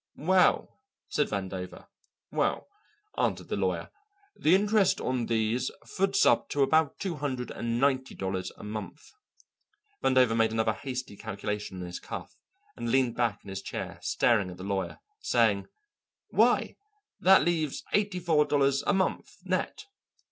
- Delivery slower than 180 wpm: Yes, average, 150 wpm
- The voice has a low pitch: Yes, low, 125 Hz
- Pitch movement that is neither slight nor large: No, wide, 7.0 semitones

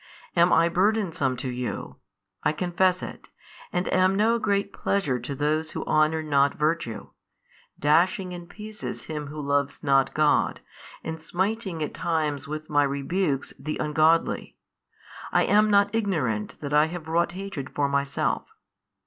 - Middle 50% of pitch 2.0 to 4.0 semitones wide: No, average, 4.4 semitones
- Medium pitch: Yes, medium, 160 Hz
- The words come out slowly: No, average, 150 wpm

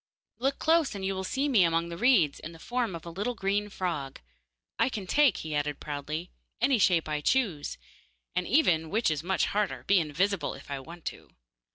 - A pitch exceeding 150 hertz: Yes, medium, 185 Hz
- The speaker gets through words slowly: No, fast, 205 wpm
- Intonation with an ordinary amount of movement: No, wide, 5.9 semitones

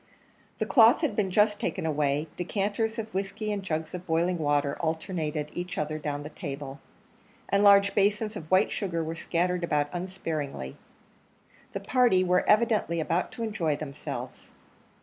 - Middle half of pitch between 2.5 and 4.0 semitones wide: No, average, 4.7 semitones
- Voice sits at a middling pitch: Yes, medium, 180 Hz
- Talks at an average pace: Yes, average, 155 wpm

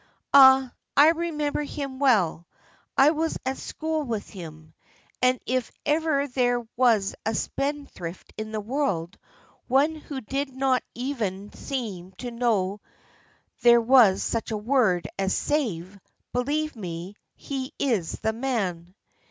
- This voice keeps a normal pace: No, slow, 130 wpm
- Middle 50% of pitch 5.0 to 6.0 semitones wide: Yes, wide, 5.6 semitones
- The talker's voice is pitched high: Yes, high, 245 Hz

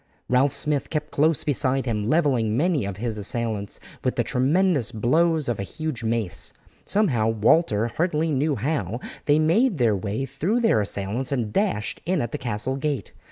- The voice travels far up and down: Yes, wide, 5.8 semitones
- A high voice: No, low, 130 Hz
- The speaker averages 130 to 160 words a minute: No, average, 170 wpm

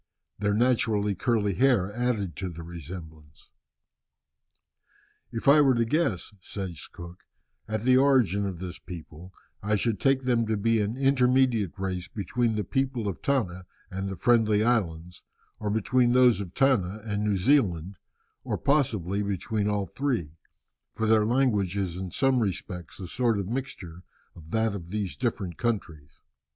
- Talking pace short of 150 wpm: No, average, 155 wpm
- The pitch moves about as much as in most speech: Yes, average, 4.9 semitones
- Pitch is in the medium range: No, low, 105 Hz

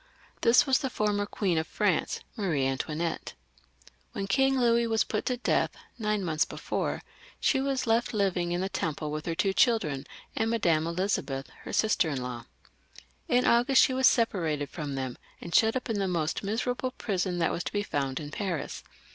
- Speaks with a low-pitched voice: No, high, 195 Hz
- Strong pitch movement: Yes, wide, 6.6 semitones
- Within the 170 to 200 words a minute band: Yes, average, 185 wpm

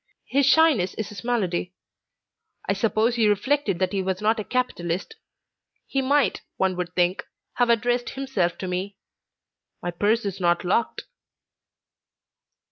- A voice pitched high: Yes, high, 205 Hz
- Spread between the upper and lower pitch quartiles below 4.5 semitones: No, average, 4.9 semitones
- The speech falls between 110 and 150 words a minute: Yes, average, 140 wpm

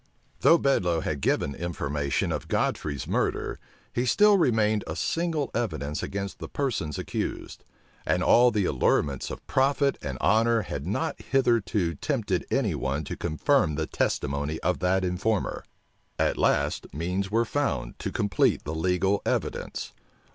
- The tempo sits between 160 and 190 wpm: No, average, 145 wpm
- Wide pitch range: Yes, wide, 7.6 semitones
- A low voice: Yes, very low, 95 Hz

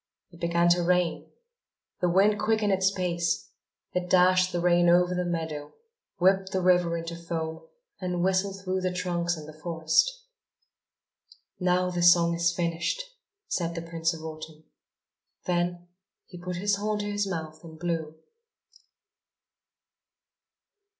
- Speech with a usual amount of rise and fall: No, narrow, 1.7 semitones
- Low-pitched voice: No, medium, 175 Hz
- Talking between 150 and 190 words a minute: No, average, 140 wpm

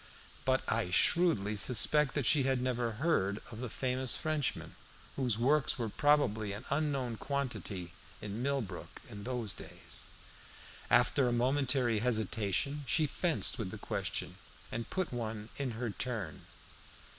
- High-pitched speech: No, low, 125 Hz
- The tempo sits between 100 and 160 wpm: Yes, average, 140 wpm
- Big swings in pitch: No, average, 4.4 semitones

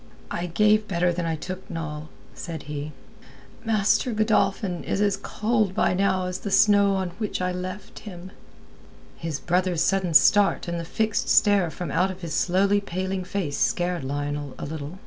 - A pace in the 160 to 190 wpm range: Yes, average, 170 wpm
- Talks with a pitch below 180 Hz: No, medium, 185 Hz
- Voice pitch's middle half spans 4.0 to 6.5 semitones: No, average, 3.1 semitones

